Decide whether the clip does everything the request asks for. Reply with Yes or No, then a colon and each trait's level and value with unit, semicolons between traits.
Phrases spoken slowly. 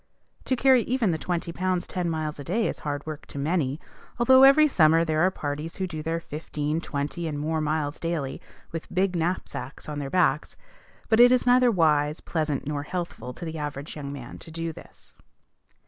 No: average, 195 wpm